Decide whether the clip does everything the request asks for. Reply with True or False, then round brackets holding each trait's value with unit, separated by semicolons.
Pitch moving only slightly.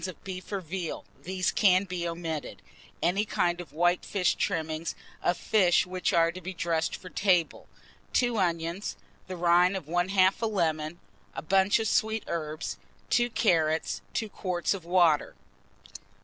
True (2.3 semitones)